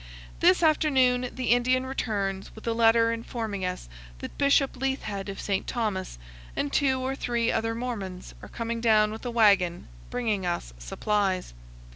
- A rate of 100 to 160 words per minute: Yes, average, 155 wpm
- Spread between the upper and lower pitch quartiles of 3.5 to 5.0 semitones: Yes, average, 4.1 semitones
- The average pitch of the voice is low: No, high, 230 Hz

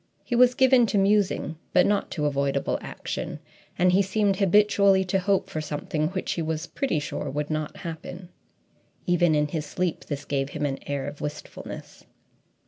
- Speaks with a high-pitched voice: No, medium, 175 Hz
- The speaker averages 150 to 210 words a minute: Yes, average, 175 wpm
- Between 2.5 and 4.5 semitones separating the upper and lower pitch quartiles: No, average, 4.9 semitones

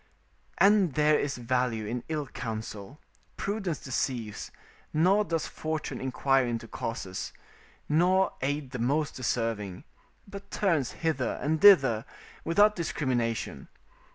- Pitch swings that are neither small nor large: No, wide, 5.7 semitones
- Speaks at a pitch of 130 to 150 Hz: Yes, medium, 140 Hz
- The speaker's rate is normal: No, slow, 115 wpm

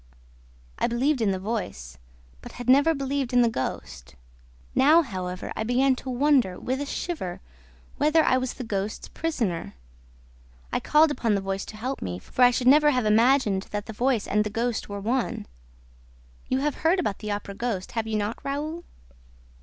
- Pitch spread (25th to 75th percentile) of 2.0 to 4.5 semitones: No, average, 5.1 semitones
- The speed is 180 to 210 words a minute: Yes, average, 185 wpm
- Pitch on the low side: No, high, 240 Hz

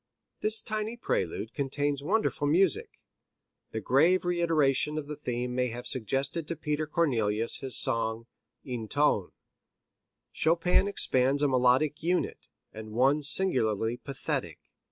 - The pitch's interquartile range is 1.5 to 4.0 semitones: No, average, 4.9 semitones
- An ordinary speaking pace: No, slow, 125 wpm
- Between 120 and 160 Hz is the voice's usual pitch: Yes, medium, 140 Hz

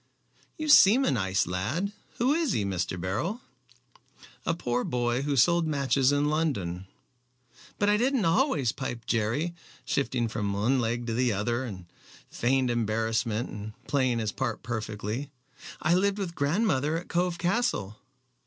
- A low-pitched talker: Yes, low, 130 Hz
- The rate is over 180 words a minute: No, average, 150 wpm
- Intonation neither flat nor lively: No, wide, 7.5 semitones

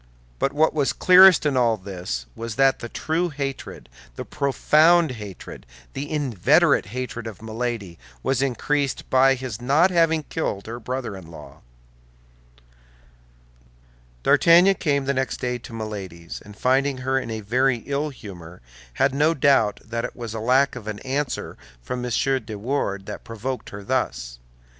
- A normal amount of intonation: Yes, average, 4.5 semitones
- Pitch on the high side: No, low, 125 Hz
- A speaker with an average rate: Yes, average, 155 wpm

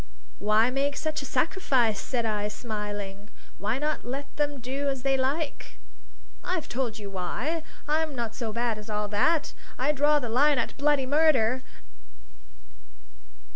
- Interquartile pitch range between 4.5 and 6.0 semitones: Yes, average, 5.0 semitones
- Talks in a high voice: Yes, very high, 260 Hz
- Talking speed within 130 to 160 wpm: Yes, average, 150 wpm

